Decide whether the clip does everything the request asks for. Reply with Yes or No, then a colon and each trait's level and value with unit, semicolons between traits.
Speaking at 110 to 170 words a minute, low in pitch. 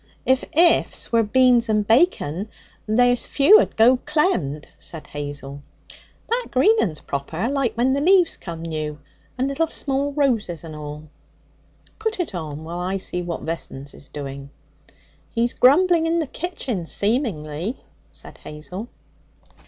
No: average, 140 wpm; high, 220 Hz